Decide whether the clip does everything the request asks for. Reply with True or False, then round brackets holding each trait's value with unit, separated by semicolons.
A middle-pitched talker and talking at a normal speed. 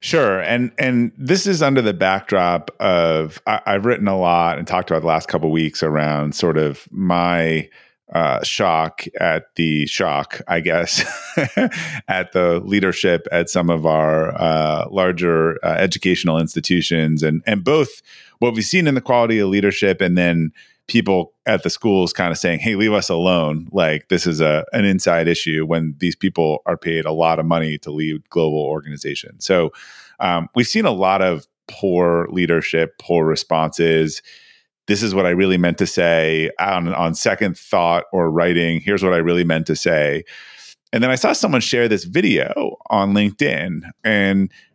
False (85 Hz; 175 wpm)